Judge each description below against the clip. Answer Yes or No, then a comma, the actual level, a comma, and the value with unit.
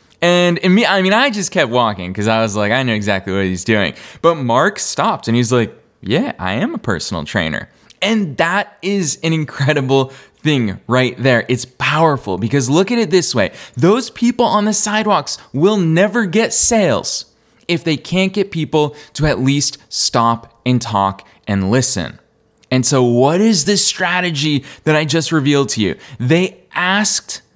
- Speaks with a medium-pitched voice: Yes, medium, 150 Hz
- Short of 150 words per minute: No, average, 180 wpm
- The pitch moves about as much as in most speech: No, wide, 7.3 semitones